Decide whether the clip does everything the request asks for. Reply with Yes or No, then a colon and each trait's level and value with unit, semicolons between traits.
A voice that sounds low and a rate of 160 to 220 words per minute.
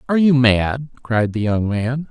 Yes: low, 125 Hz; average, 200 wpm